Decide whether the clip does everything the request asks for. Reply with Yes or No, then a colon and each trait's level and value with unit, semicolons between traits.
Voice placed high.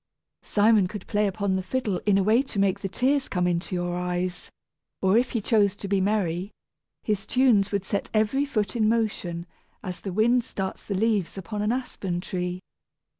Yes: high, 200 Hz